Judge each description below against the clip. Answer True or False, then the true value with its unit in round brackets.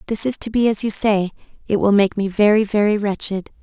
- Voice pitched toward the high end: True (205 Hz)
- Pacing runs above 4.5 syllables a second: True (5.9 syllables/s)